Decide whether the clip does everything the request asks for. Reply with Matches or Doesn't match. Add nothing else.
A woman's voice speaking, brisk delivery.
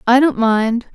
Doesn't match